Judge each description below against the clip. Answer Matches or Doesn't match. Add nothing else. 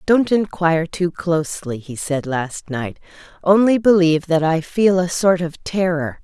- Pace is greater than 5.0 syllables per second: Doesn't match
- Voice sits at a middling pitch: Matches